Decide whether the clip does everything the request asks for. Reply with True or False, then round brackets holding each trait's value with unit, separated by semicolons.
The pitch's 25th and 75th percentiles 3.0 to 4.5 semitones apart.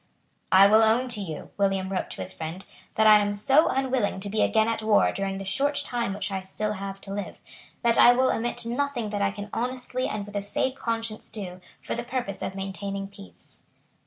True (3.4 semitones)